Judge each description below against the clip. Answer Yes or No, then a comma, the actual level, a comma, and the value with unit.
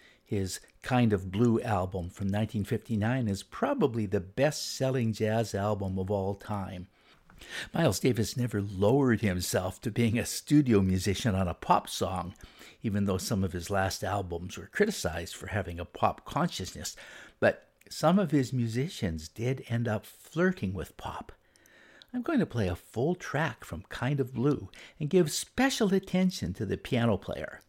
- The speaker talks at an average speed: Yes, average, 165 wpm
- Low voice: Yes, low, 110 Hz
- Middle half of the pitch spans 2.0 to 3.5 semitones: No, average, 5.3 semitones